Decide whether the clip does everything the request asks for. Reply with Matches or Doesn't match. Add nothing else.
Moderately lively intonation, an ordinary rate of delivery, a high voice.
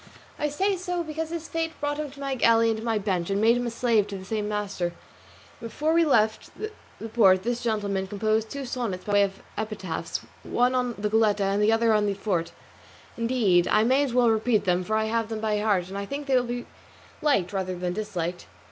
Doesn't match